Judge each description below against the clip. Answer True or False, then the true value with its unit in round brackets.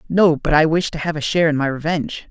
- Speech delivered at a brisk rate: True (285 wpm)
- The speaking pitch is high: False (155 Hz)